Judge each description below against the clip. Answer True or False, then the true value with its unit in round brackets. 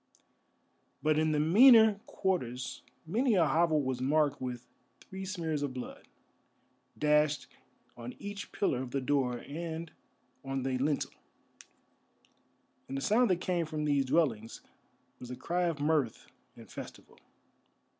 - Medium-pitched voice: True (150 Hz)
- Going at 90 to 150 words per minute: True (135 wpm)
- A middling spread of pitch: True (4.6 semitones)